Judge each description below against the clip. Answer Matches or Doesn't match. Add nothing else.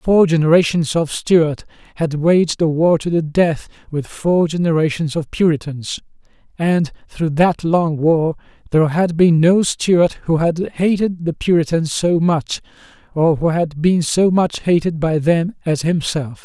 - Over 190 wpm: Doesn't match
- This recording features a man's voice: Matches